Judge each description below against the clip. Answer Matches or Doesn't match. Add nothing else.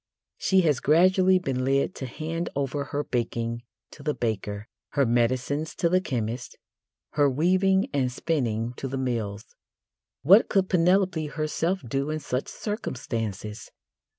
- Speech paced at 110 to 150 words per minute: Matches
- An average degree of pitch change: Doesn't match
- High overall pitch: Doesn't match